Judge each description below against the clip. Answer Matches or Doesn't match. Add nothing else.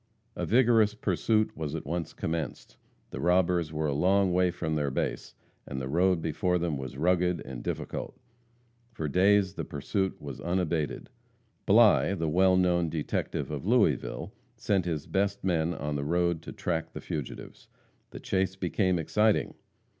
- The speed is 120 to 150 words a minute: Doesn't match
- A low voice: Matches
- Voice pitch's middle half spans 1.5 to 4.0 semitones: Matches